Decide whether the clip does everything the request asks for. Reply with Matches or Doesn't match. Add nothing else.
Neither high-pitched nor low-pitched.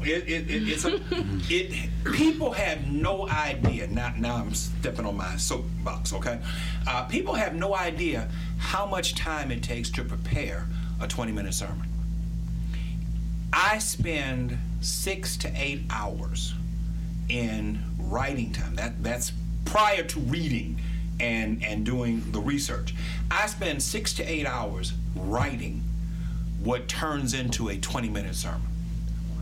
Matches